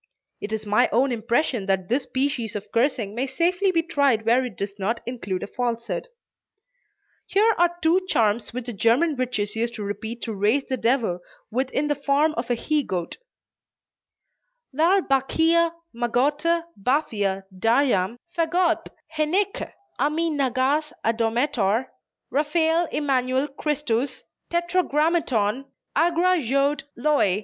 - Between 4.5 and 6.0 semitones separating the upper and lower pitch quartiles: Yes, average, 5.2 semitones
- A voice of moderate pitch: No, very high, 260 Hz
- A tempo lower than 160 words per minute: Yes, slow, 135 wpm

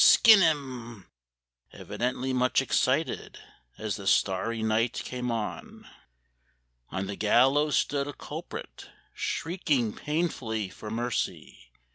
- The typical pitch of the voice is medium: No, low, 125 Hz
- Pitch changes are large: No, average, 4.4 semitones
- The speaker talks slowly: Yes, slow, 105 wpm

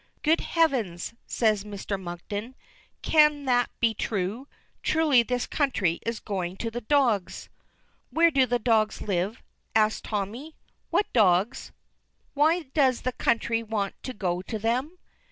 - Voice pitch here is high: Yes, high, 230 Hz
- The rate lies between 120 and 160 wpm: Yes, slow, 135 wpm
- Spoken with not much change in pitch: No, average, 4.7 semitones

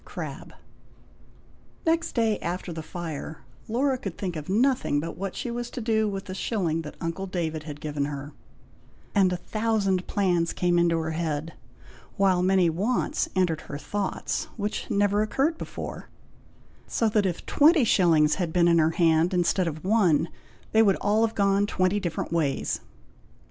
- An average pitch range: Yes, average, 4.3 semitones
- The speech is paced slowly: No, average, 165 wpm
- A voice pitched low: No, medium, 185 Hz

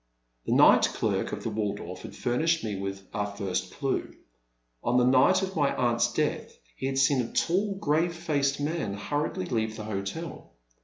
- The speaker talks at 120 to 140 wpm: No, average, 175 wpm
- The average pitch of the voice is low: Yes, low, 125 Hz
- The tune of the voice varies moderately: No, wide, 7.0 semitones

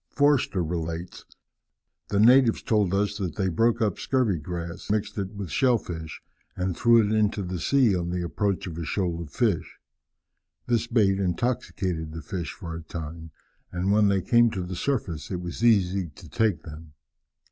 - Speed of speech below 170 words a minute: No, average, 180 wpm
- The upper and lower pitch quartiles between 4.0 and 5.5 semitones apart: Yes, average, 4.3 semitones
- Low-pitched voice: Yes, very low, 95 Hz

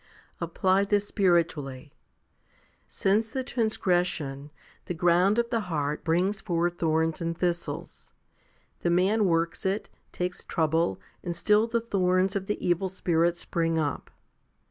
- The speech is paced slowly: Yes, slow, 130 wpm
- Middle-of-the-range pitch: Yes, medium, 175 Hz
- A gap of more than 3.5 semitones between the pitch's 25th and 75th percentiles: No, average, 3.2 semitones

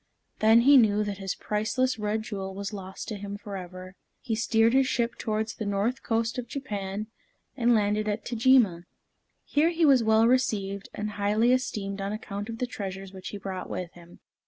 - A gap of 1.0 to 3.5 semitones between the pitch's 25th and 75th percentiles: Yes, average, 2.9 semitones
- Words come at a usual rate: Yes, average, 185 wpm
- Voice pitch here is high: Yes, high, 215 Hz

